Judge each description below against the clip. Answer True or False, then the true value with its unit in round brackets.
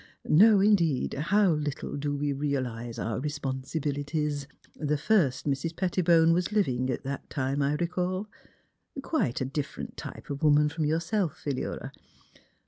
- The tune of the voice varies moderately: True (3.5 semitones)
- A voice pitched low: False (150 Hz)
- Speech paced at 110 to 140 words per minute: True (135 wpm)